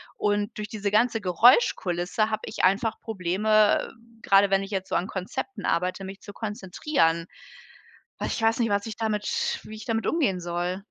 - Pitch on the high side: Yes, high, 205 Hz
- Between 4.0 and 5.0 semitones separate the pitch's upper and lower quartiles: No, average, 2.8 semitones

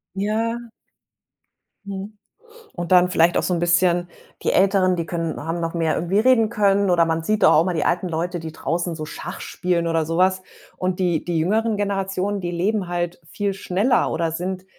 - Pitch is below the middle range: No, medium, 180 Hz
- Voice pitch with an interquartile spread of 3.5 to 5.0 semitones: No, average, 2.7 semitones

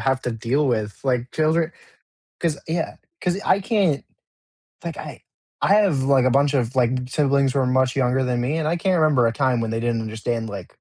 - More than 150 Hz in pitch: No, low, 130 Hz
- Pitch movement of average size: Yes, average, 4.3 semitones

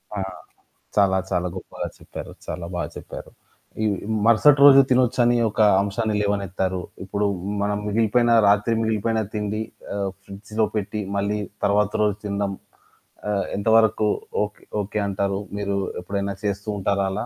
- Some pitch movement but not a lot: No, narrow, 1.8 semitones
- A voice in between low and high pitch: No, low, 105 Hz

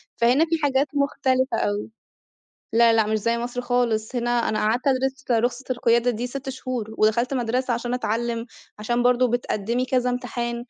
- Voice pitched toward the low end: No, high, 245 Hz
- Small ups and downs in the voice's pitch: Yes, narrow, 1.6 semitones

